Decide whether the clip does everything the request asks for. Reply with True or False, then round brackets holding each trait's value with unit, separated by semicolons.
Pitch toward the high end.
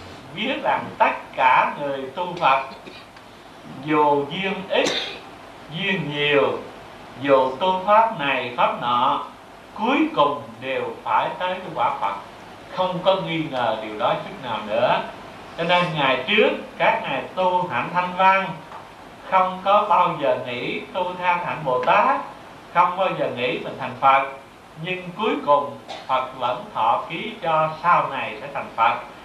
False (175 Hz)